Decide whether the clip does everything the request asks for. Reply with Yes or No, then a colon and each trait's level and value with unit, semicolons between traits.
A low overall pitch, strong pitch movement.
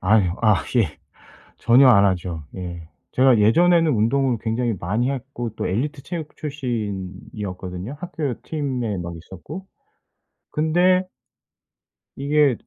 Yes: low, 120 Hz; wide, 7.0 semitones